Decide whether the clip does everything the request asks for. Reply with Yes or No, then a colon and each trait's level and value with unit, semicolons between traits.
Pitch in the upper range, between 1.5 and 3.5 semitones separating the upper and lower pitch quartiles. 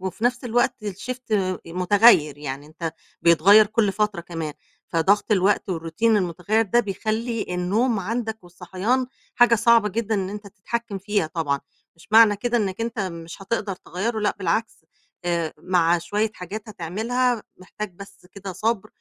No: high, 205 Hz; average, 4.2 semitones